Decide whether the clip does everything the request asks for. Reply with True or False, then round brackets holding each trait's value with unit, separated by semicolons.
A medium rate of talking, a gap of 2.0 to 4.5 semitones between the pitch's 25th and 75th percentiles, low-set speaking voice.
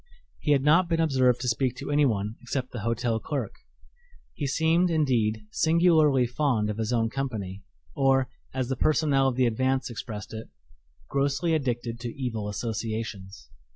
True (155 wpm; 4.1 semitones; 130 Hz)